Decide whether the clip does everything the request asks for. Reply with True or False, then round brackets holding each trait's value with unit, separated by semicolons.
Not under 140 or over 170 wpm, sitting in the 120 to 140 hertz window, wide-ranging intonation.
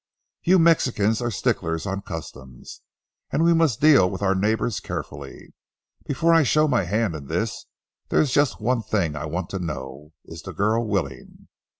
False (165 wpm; 100 Hz; 7.6 semitones)